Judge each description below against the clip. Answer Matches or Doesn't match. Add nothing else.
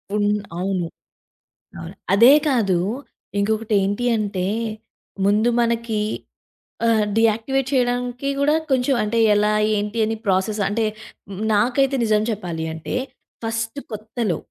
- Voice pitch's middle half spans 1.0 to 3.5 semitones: Matches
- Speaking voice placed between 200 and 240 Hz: Matches